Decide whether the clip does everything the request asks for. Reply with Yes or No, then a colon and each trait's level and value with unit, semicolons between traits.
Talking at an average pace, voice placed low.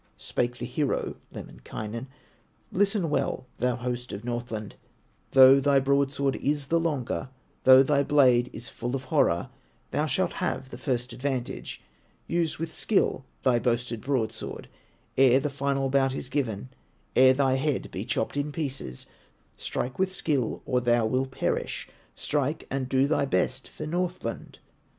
Yes: average, 150 wpm; low, 130 Hz